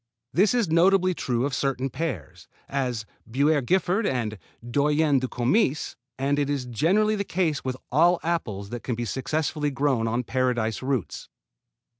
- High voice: No, medium, 140 Hz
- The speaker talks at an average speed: Yes, average, 155 wpm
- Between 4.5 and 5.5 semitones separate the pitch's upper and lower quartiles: Yes, average, 5.0 semitones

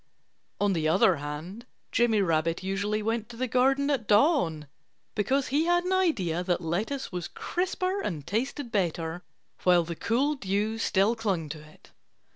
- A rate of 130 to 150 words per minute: No, average, 160 wpm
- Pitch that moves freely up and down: Yes, wide, 7.0 semitones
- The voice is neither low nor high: No, high, 205 Hz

